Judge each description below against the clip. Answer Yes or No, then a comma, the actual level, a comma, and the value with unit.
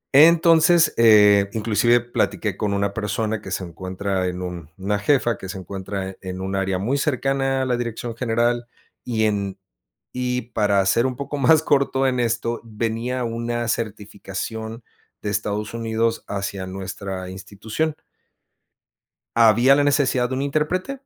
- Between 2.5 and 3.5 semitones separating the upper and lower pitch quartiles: No, average, 4.2 semitones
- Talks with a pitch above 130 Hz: No, low, 115 Hz